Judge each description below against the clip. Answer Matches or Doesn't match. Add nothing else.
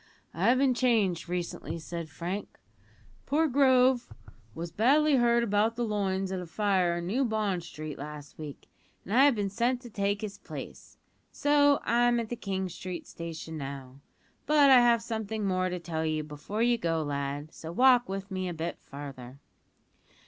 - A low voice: Doesn't match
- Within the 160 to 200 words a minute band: Matches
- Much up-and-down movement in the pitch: Matches